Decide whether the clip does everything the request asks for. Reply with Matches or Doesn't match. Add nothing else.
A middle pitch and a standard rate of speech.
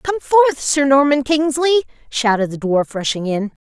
Doesn't match